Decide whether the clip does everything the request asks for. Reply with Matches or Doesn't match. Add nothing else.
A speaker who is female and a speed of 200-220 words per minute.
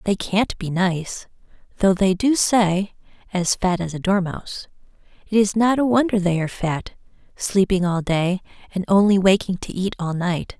Doesn't match